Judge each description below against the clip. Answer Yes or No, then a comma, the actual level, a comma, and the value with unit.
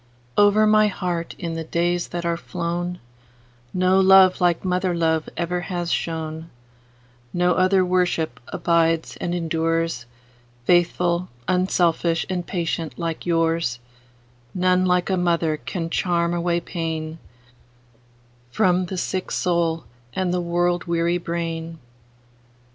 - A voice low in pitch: No, medium, 170 Hz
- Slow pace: Yes, slow, 110 wpm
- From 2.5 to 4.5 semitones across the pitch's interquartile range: Yes, average, 2.8 semitones